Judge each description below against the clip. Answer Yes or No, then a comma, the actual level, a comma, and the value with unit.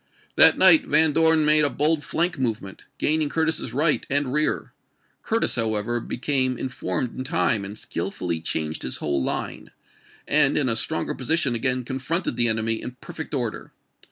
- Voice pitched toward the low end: Yes, low, 130 Hz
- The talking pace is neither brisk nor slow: Yes, average, 160 wpm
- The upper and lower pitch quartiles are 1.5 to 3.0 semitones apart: No, average, 5.3 semitones